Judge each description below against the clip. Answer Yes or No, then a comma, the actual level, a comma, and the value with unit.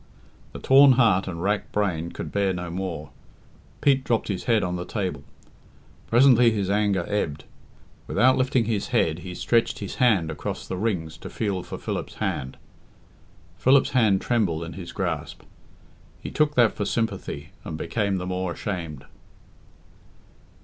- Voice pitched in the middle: No, low, 100 Hz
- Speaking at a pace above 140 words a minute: Yes, average, 155 wpm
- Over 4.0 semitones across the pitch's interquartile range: Yes, average, 4.8 semitones